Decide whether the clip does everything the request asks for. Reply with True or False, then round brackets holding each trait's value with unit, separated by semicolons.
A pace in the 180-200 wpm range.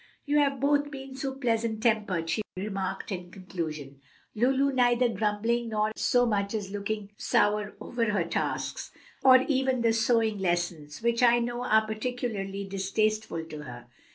False (155 wpm)